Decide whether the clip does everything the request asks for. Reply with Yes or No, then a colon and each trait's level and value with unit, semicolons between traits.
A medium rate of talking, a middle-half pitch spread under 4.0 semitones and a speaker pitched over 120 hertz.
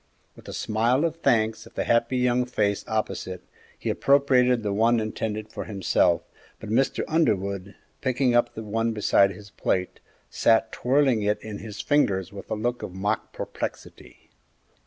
No: average, 160 wpm; average, 3.4 semitones; low, 110 Hz